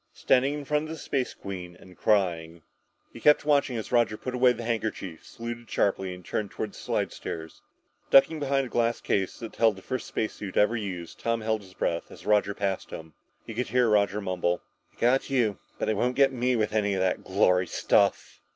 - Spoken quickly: Yes, fast, 210 wpm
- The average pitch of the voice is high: No, low, 110 Hz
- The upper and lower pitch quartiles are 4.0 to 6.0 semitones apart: Yes, average, 4.6 semitones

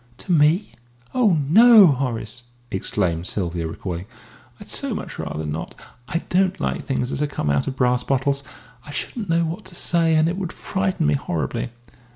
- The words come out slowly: No, average, 180 wpm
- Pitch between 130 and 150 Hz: Yes, medium, 140 Hz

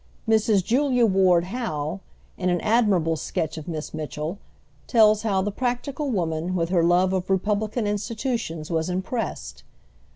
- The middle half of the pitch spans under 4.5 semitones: No, average, 4.8 semitones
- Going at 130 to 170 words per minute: Yes, average, 140 wpm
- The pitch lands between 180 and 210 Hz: Yes, high, 190 Hz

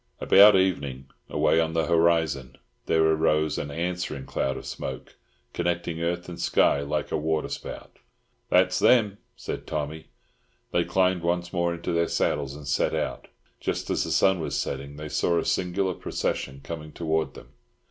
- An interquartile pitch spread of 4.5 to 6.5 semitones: No, average, 2.8 semitones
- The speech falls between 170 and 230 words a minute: No, average, 160 wpm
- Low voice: Yes, very low, 80 Hz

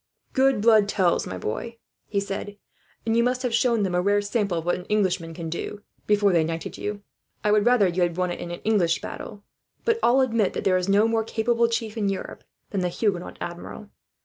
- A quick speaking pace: Yes, fast, 225 wpm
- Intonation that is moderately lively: Yes, average, 4.1 semitones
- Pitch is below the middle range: No, high, 205 Hz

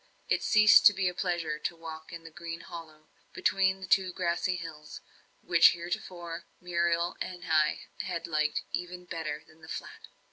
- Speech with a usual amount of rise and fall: No, narrow, 1.8 semitones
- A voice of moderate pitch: Yes, medium, 170 Hz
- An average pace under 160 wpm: No, average, 170 wpm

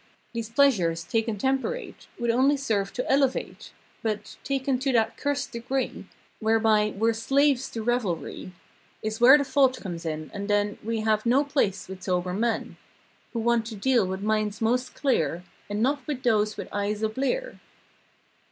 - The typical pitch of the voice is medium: No, high, 225 Hz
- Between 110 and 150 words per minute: No, average, 165 wpm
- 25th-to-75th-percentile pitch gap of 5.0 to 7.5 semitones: No, average, 4.1 semitones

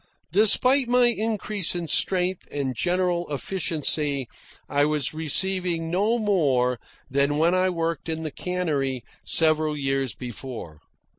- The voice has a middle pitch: Yes, medium, 160 Hz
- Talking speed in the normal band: No, slow, 125 wpm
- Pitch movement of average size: Yes, average, 4.8 semitones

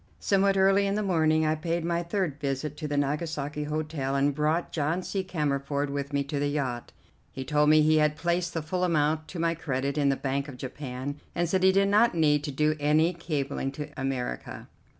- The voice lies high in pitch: No, medium, 150 Hz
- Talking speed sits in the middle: No, fast, 210 wpm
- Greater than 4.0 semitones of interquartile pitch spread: No, average, 3.2 semitones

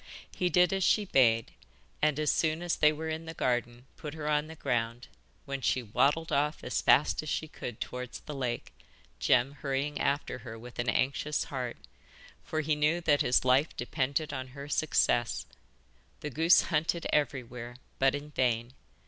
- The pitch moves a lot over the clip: No, average, 3.8 semitones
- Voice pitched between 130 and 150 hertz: Yes, medium, 140 Hz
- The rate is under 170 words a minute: No, average, 175 wpm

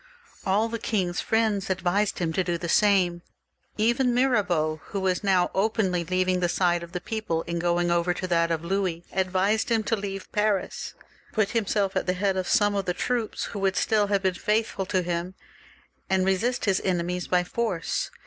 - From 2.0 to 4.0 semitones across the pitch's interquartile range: Yes, average, 2.9 semitones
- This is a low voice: No, high, 190 Hz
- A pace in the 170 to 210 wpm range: Yes, average, 190 wpm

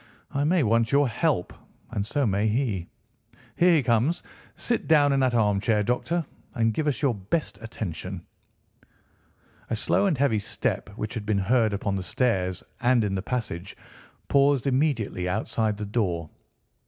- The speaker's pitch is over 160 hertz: No, low, 115 Hz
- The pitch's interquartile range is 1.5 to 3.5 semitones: No, average, 5.3 semitones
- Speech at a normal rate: Yes, average, 160 wpm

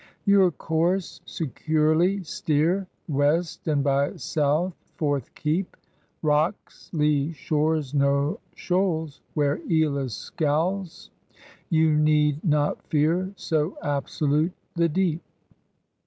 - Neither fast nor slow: No, slow, 95 wpm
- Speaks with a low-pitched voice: No, medium, 155 Hz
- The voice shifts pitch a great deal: No, average, 2.8 semitones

